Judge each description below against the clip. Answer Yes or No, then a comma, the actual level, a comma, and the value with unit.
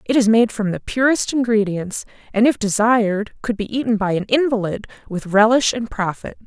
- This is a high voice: Yes, high, 220 Hz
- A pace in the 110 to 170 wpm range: No, average, 185 wpm